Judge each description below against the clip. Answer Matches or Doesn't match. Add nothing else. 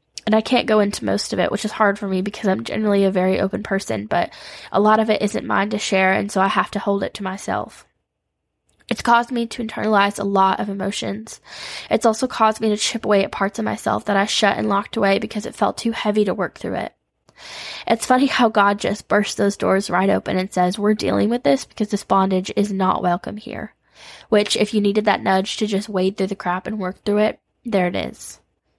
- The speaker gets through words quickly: Matches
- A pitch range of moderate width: Doesn't match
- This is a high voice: Matches